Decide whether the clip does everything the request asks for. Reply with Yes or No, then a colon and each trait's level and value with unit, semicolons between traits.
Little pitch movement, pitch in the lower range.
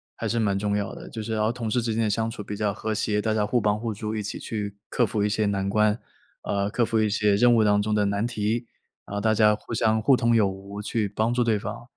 Yes: narrow, 1.7 semitones; low, 110 Hz